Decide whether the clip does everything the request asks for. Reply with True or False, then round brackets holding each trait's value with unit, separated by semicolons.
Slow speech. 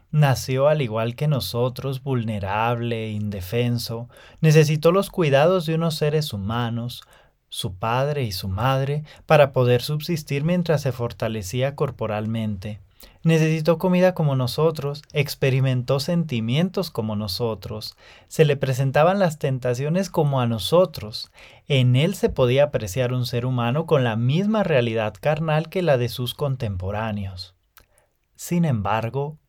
True (125 wpm)